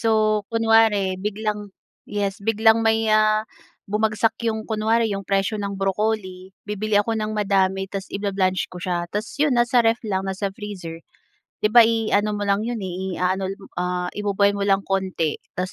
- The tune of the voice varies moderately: No, narrow, 2.3 semitones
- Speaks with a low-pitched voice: No, high, 205 Hz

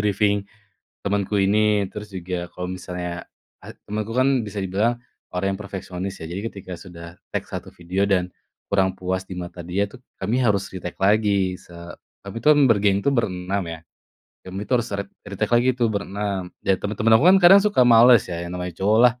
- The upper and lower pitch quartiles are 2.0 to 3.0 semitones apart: Yes, narrow, 2.6 semitones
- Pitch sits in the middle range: No, low, 100 Hz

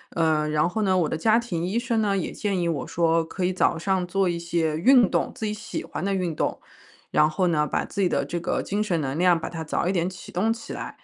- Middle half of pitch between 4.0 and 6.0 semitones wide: No, average, 3.3 semitones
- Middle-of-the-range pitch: Yes, medium, 175 Hz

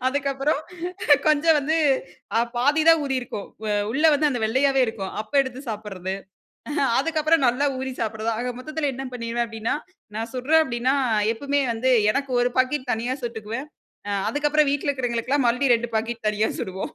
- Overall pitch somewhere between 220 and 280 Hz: Yes, very high, 255 Hz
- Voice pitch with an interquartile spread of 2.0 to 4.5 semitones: Yes, average, 3.8 semitones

